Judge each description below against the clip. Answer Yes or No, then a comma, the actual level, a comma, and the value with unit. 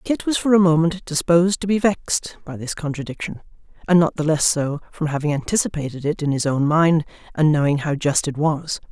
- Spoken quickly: Yes, fast, 210 wpm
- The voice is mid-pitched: Yes, medium, 160 Hz